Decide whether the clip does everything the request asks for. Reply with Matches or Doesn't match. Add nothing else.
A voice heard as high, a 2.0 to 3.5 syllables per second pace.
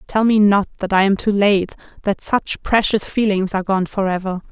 Doesn't match